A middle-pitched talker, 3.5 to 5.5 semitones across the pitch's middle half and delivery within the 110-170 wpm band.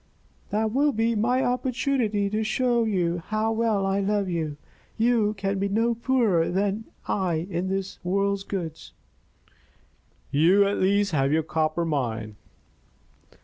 No: high, 200 Hz; average, 4.2 semitones; slow, 135 wpm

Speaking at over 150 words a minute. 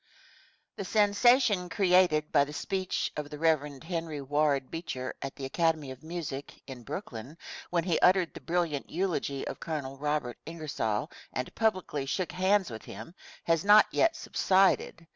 Yes: average, 160 wpm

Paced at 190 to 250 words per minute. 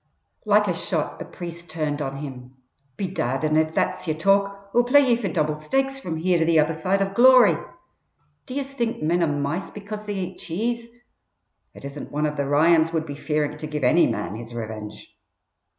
Yes: average, 200 wpm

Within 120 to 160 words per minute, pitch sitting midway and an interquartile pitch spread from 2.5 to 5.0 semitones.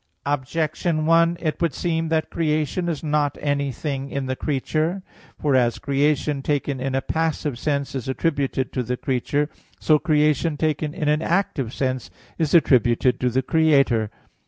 Yes: average, 155 wpm; medium, 145 Hz; average, 3.0 semitones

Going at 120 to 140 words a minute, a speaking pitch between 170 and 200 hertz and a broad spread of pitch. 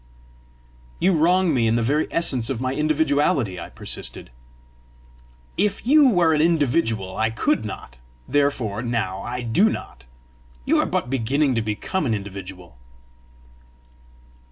No: slow, 135 wpm; low, 130 Hz; wide, 6.3 semitones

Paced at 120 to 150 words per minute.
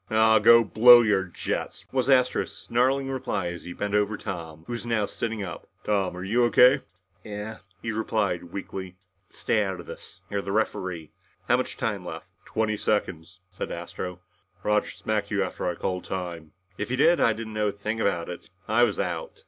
No: average, 195 wpm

